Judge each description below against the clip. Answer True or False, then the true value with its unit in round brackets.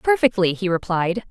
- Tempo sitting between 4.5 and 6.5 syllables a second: True (4.9 syllables/s)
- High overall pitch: True (200 Hz)